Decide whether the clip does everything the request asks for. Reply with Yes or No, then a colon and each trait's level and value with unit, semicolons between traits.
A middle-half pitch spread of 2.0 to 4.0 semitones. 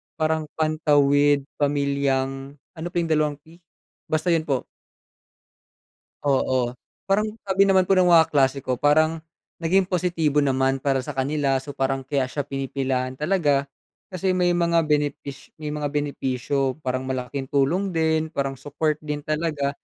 Yes: average, 2.9 semitones